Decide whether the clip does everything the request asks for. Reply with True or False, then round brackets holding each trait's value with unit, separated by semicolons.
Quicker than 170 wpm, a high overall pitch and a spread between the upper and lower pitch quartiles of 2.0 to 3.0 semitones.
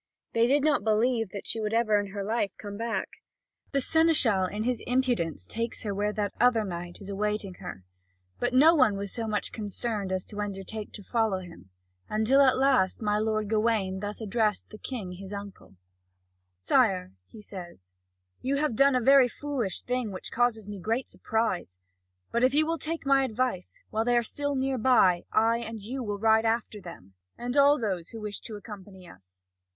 False (190 wpm; 220 Hz; 3.8 semitones)